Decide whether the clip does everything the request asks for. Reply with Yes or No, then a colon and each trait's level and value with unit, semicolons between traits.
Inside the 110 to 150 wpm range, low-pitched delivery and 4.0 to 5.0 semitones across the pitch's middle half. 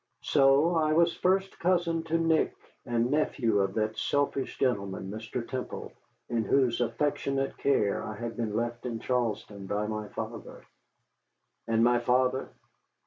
Yes: average, 140 wpm; low, 125 Hz; average, 4.4 semitones